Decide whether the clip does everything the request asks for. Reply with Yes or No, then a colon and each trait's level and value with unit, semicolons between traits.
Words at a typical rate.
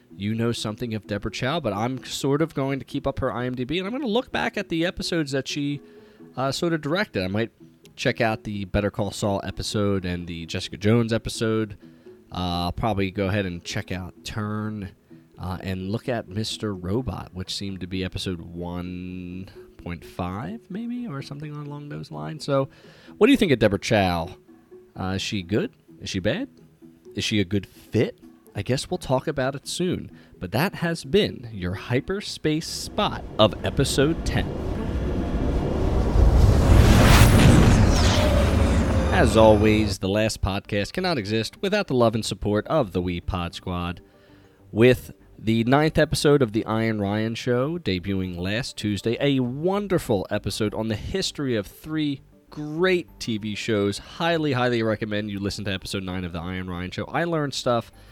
Yes: average, 170 wpm